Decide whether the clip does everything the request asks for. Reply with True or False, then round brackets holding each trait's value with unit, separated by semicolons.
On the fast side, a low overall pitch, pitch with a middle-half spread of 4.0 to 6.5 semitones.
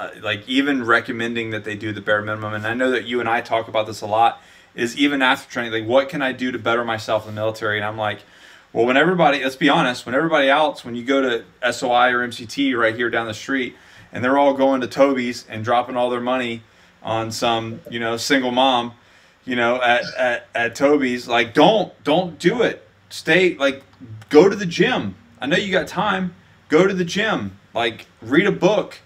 False (225 wpm; 120 Hz; 3.5 semitones)